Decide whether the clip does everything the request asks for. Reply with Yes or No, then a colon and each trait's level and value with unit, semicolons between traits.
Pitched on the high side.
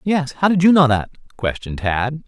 No: medium, 140 Hz